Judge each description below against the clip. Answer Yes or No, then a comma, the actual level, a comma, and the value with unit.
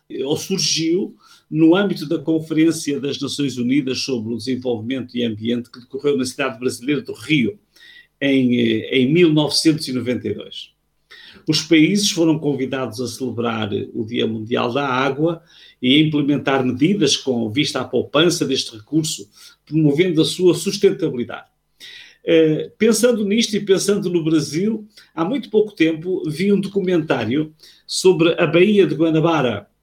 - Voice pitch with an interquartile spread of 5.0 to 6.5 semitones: Yes, wide, 5.5 semitones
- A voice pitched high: No, medium, 155 Hz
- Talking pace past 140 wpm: No, average, 135 wpm